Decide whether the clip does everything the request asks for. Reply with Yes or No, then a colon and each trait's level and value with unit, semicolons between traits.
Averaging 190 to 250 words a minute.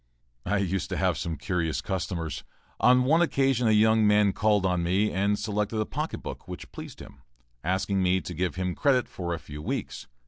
Yes: average, 200 wpm